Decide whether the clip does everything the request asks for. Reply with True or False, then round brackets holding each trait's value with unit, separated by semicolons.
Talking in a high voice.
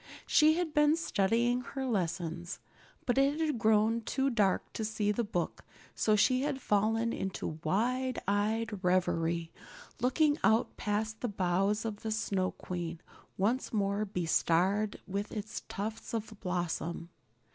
True (215 Hz)